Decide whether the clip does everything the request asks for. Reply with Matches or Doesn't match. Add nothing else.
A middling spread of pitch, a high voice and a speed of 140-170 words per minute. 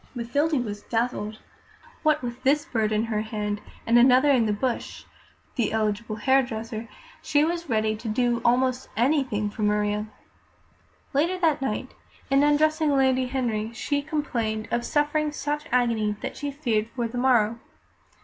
Matches